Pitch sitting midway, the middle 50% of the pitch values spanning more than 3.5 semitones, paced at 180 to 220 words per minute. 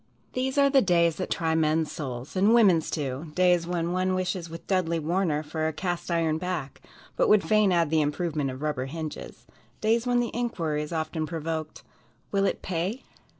No: medium, 170 Hz; average, 3.2 semitones; average, 190 wpm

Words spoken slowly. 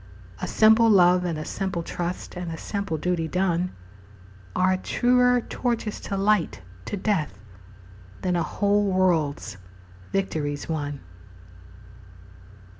Yes: slow, 115 wpm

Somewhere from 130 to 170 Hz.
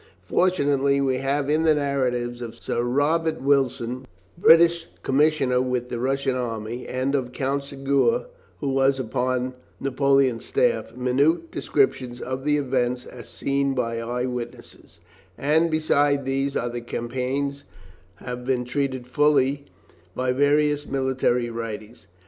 Yes: low, 135 Hz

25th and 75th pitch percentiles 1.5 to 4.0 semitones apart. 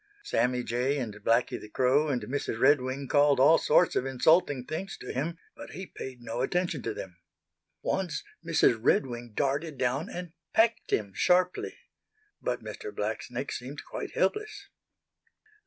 No: average, 5.1 semitones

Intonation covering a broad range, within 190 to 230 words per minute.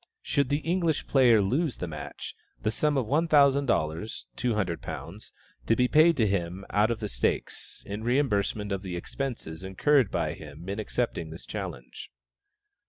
No: wide, 6.7 semitones; average, 165 wpm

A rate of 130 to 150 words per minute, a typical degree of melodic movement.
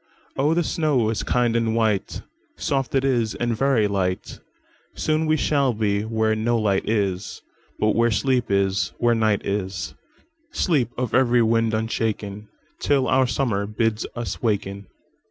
Yes: slow, 135 wpm; average, 4.0 semitones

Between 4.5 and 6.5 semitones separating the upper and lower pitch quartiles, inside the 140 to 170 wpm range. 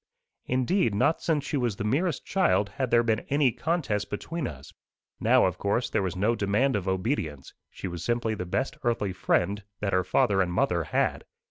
No: wide, 5.6 semitones; average, 195 wpm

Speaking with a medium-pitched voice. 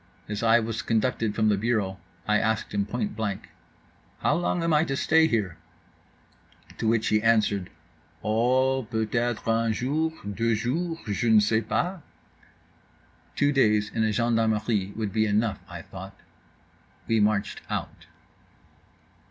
No: low, 110 Hz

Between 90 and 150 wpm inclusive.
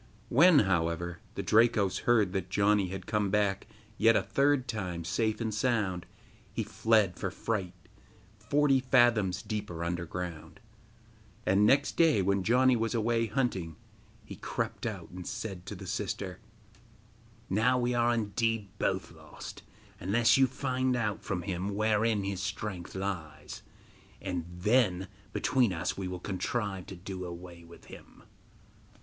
Yes: average, 145 wpm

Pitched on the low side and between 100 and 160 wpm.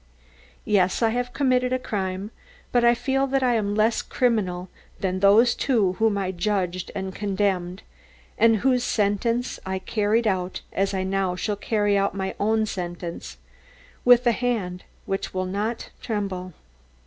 No: high, 205 Hz; average, 155 wpm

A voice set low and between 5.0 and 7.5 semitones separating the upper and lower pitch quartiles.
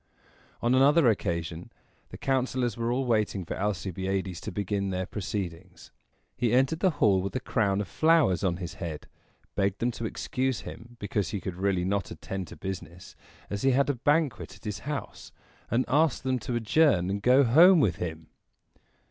Yes: low, 105 Hz; wide, 5.5 semitones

